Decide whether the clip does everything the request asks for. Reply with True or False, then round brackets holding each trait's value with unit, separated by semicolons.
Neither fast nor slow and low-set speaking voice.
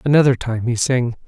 True (190 wpm; 125 Hz)